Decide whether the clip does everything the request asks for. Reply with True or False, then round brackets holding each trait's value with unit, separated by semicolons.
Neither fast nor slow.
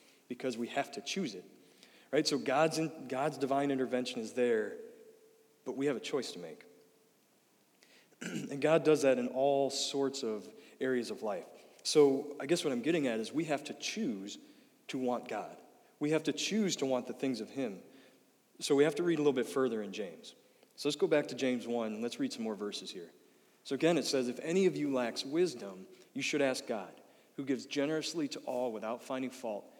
False (210 wpm)